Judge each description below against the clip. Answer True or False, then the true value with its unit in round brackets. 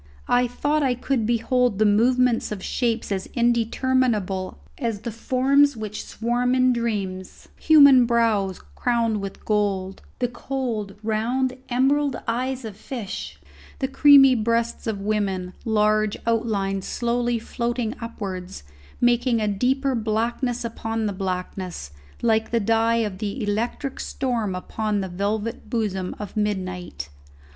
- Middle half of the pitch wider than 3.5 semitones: False (3.2 semitones)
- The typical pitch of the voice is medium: False (230 Hz)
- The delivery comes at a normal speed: False (130 wpm)